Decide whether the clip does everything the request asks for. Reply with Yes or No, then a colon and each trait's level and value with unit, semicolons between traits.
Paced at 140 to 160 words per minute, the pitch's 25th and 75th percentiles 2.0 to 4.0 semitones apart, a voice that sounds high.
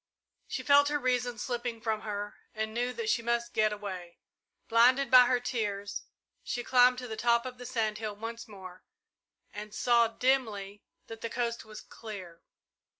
No: average, 170 wpm; average, 2.7 semitones; high, 230 Hz